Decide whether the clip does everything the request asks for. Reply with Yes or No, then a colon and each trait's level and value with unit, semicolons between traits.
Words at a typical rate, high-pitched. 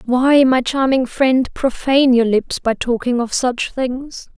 Yes: average, 165 wpm; very high, 255 Hz